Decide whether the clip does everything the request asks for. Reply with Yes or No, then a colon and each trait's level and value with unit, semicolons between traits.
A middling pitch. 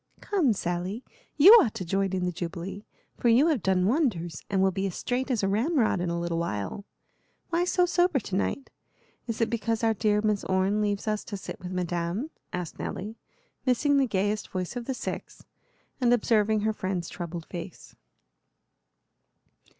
No: high, 205 Hz